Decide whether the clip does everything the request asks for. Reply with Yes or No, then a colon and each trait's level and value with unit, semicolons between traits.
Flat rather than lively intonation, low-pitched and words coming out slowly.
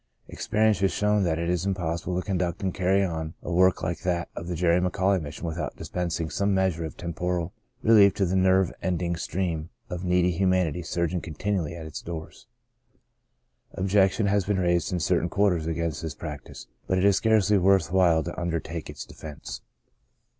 No: narrow, 2.3 semitones; very low, 90 Hz; average, 180 wpm